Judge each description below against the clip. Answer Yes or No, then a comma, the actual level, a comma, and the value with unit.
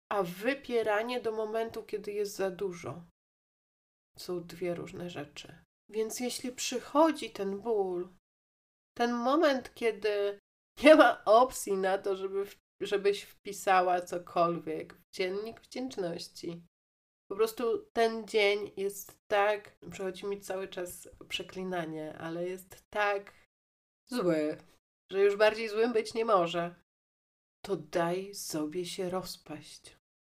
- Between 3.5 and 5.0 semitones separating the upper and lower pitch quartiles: Yes, average, 4.1 semitones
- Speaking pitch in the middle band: No, high, 195 Hz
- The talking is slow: No, average, 120 wpm